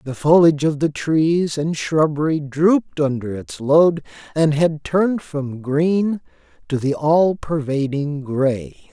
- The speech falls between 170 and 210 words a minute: No, average, 140 wpm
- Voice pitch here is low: No, medium, 155 Hz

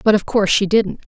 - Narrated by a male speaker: No, female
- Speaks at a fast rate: Yes, fast, 260 wpm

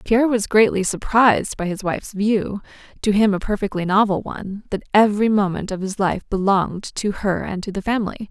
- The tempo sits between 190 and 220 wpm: Yes, average, 195 wpm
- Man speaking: No, female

